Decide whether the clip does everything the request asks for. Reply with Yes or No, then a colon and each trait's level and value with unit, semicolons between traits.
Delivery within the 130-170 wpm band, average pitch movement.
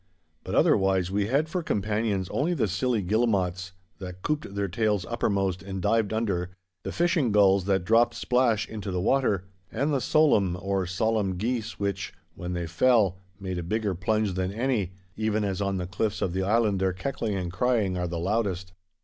No: average, 185 wpm; average, 3.4 semitones